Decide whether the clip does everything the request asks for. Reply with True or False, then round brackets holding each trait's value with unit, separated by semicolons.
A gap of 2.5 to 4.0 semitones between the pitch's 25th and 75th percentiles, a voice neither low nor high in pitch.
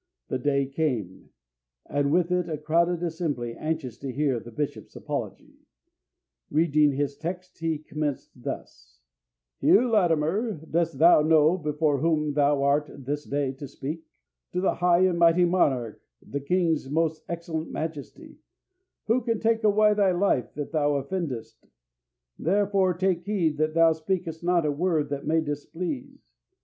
True (3.6 semitones; 160 Hz)